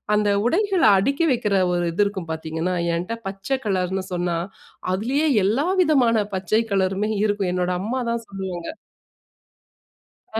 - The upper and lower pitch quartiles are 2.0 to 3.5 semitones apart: No, average, 4.4 semitones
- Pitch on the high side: Yes, high, 200 Hz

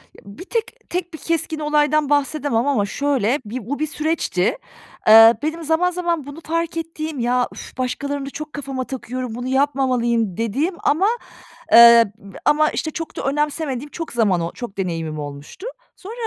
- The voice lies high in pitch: Yes, very high, 280 Hz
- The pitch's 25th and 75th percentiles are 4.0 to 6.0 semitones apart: Yes, average, 4.9 semitones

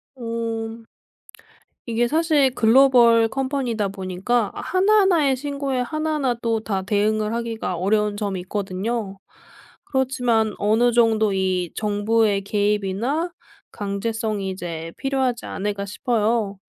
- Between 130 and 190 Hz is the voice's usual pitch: No, high, 225 Hz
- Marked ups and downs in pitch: No, average, 3.6 semitones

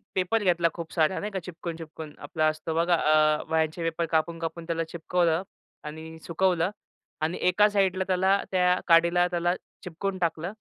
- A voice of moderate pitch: Yes, medium, 170 Hz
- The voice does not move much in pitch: Yes, narrow, 2.1 semitones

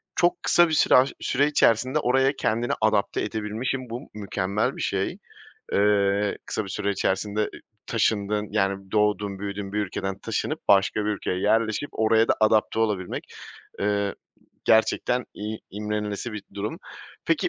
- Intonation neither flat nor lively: No, narrow, 2.0 semitones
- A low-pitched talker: Yes, low, 105 Hz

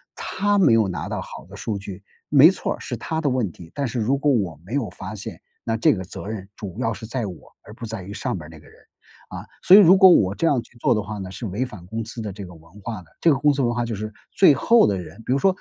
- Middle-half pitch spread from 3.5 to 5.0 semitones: No, wide, 5.6 semitones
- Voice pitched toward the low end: Yes, low, 110 Hz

